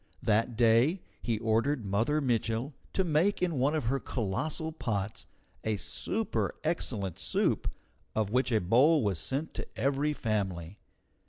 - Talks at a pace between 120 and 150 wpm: Yes, average, 145 wpm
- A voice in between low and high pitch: No, low, 120 Hz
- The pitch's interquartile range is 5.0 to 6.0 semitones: Yes, wide, 5.6 semitones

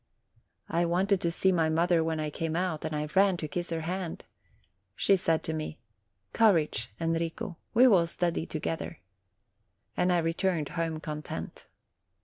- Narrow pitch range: Yes, narrow, 2.1 semitones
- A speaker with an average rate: Yes, average, 155 wpm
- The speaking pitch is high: No, medium, 165 Hz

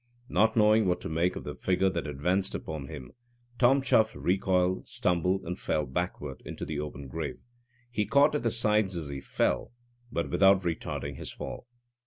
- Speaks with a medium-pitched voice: No, very low, 90 Hz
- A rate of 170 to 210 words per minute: Yes, average, 180 wpm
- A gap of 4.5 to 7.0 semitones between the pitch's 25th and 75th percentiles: Yes, average, 5.3 semitones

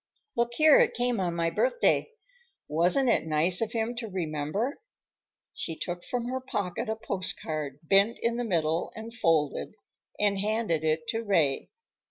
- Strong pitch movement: Yes, wide, 6.2 semitones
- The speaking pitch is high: Yes, high, 200 Hz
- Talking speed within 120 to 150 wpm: No, average, 160 wpm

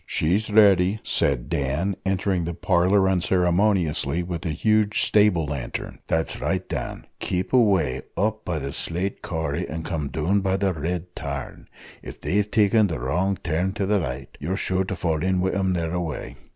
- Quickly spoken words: No, average, 170 wpm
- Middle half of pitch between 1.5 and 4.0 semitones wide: Yes, average, 3.4 semitones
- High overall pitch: No, very low, 90 Hz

